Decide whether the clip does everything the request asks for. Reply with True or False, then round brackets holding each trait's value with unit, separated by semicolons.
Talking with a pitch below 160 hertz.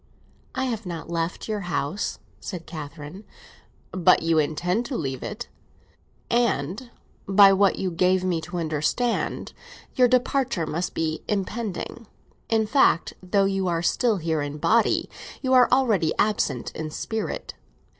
False (185 Hz)